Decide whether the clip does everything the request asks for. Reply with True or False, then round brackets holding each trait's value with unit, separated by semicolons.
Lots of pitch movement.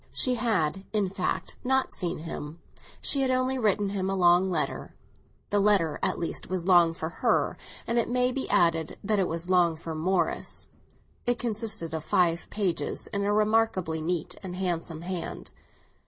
False (4.2 semitones)